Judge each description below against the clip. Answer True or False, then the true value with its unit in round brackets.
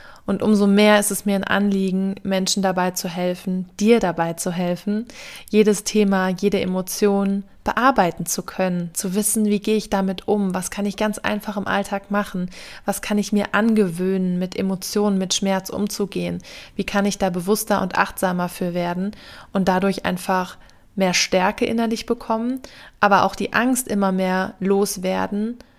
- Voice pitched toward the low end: False (200 Hz)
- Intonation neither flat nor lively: False (2.0 semitones)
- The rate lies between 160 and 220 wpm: True (165 wpm)